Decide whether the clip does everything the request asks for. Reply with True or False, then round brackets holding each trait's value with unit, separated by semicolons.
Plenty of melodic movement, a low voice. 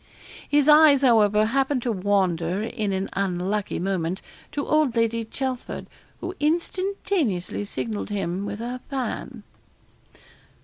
False (5.9 semitones; 225 Hz)